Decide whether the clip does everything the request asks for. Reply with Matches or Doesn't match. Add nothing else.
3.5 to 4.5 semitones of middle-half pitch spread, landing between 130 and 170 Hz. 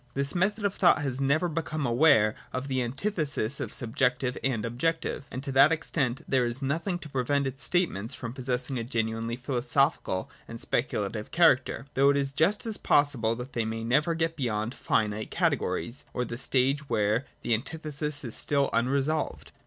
Matches